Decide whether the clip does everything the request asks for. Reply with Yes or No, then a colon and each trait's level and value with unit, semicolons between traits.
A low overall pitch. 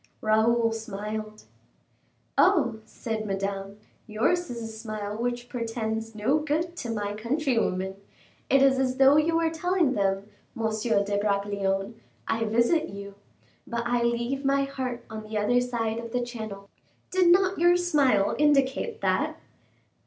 No: high, 235 Hz